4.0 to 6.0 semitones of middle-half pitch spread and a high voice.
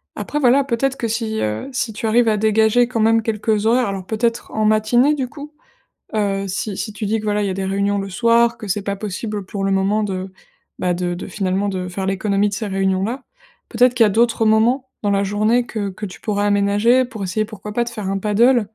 No: average, 2.9 semitones; high, 215 Hz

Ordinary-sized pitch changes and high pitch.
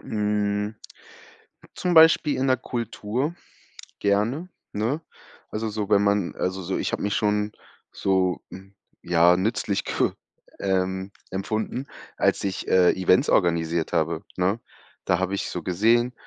No: average, 3.0 semitones; low, 100 Hz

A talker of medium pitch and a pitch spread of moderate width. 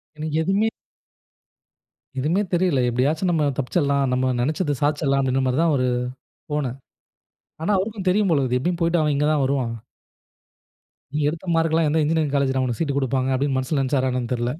Yes: medium, 145 Hz; average, 3.7 semitones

